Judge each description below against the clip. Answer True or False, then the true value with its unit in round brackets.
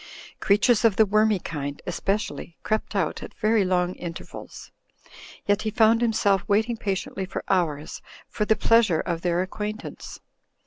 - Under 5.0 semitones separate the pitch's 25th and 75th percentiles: True (3.4 semitones)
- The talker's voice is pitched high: True (200 Hz)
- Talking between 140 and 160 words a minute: True (150 wpm)